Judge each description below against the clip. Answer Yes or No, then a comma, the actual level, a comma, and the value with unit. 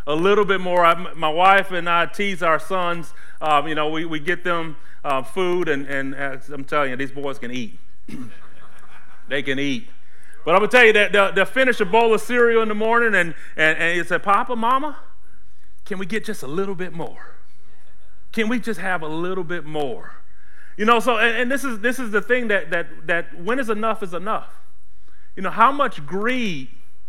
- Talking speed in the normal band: No, fast, 215 wpm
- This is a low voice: No, medium, 180 Hz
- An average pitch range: No, wide, 6.1 semitones